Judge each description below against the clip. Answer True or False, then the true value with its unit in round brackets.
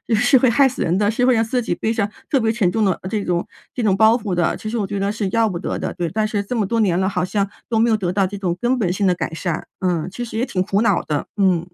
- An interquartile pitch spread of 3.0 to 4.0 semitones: True (3.6 semitones)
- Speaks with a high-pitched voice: True (205 Hz)